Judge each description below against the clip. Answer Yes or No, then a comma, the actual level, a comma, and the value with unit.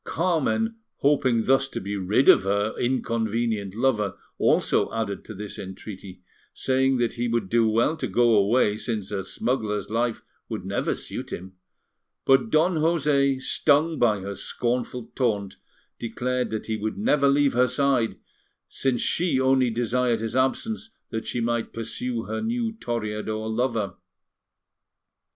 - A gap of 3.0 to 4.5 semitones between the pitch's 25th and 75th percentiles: Yes, average, 3.6 semitones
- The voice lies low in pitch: Yes, low, 120 Hz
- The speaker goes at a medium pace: Yes, average, 145 wpm